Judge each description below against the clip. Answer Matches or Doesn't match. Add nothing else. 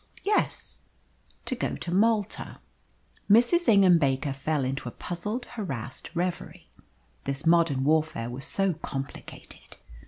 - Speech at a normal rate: Doesn't match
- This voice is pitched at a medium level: Matches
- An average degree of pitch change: Doesn't match